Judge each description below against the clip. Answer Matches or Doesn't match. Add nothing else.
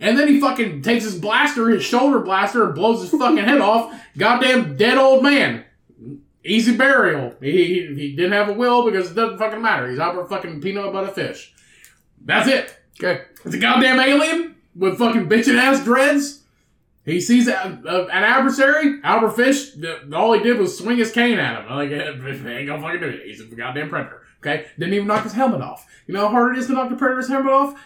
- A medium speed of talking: Doesn't match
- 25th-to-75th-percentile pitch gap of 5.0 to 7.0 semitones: Matches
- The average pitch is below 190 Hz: Doesn't match